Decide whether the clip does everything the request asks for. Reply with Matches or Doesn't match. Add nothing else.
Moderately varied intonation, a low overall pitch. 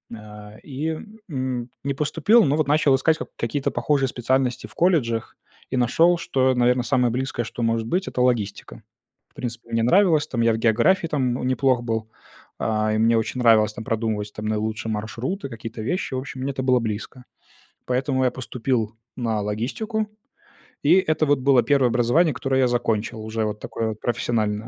Matches